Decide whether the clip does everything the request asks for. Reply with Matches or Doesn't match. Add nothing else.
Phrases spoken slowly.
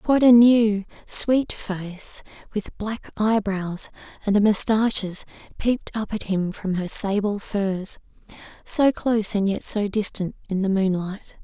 Matches